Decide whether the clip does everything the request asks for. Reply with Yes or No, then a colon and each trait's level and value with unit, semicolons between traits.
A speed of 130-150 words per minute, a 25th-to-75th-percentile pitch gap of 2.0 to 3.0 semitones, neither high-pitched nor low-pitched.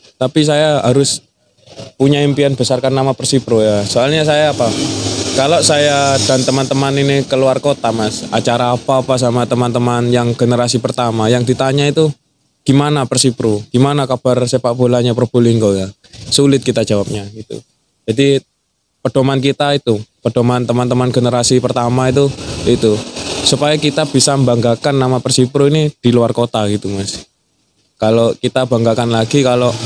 No: fast, 140 wpm; narrow, 2.6 semitones; low, 125 Hz